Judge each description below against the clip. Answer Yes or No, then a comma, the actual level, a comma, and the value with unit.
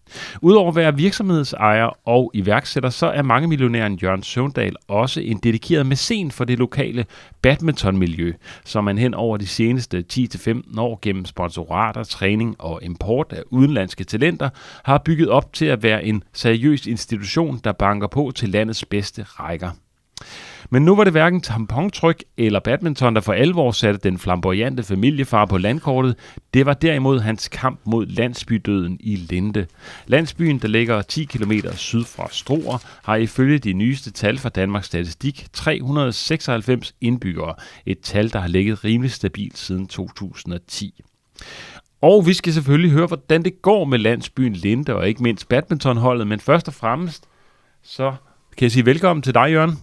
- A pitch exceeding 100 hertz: Yes, low, 120 Hz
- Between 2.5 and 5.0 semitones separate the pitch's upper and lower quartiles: No, wide, 5.4 semitones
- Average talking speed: Yes, average, 160 wpm